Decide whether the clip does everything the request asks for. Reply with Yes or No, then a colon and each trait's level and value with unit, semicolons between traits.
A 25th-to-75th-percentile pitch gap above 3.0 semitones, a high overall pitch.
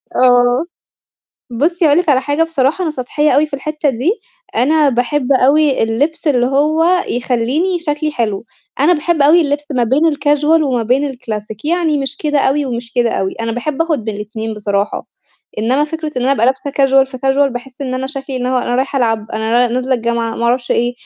Yes: average, 3.6 semitones; very high, 265 Hz